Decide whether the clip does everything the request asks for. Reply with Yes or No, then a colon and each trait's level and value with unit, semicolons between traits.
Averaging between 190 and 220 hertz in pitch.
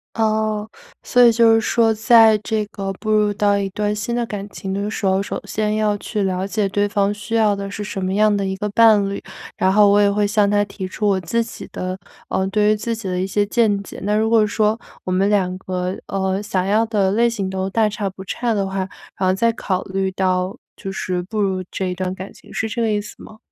Yes: high, 205 Hz